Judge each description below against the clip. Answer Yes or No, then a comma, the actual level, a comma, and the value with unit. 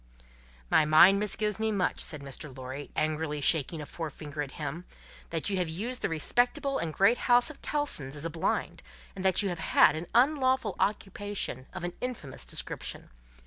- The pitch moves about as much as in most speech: No, wide, 6.0 semitones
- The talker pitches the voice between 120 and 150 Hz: No, medium, 170 Hz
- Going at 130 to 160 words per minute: No, average, 180 wpm